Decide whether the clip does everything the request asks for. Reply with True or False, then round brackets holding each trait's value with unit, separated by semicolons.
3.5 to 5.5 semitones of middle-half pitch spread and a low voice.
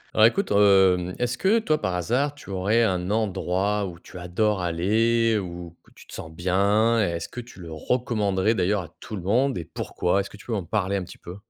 True (4.0 semitones; 100 Hz)